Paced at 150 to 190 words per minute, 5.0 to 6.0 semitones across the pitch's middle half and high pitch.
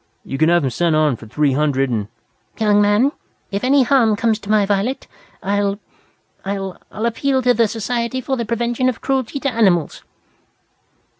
Yes: average, 180 wpm; wide, 5.6 semitones; high, 210 Hz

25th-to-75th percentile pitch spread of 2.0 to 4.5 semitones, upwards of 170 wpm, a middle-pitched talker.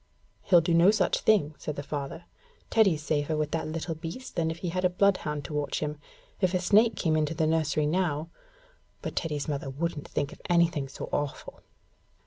Yes: average, 3.1 semitones; average, 200 wpm; medium, 160 Hz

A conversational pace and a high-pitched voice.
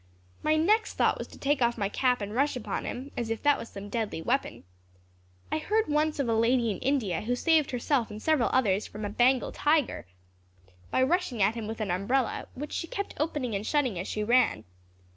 No: fast, 215 wpm; high, 245 Hz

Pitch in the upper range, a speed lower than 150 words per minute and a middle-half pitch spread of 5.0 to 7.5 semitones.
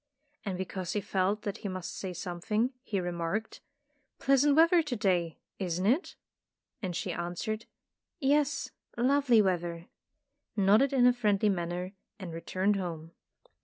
Yes: high, 200 Hz; average, 140 wpm; wide, 5.6 semitones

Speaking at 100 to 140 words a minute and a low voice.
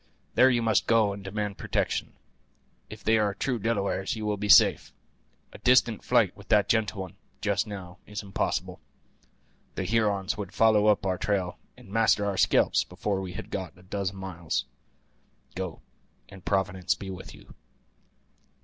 No: average, 165 wpm; low, 100 Hz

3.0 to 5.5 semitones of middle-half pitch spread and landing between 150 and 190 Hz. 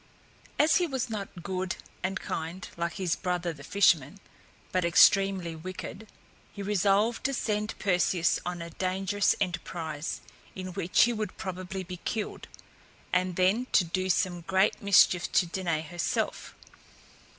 No: narrow, 2.4 semitones; medium, 185 Hz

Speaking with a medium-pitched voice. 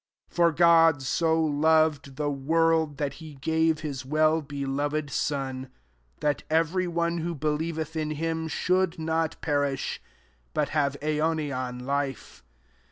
Yes: medium, 155 Hz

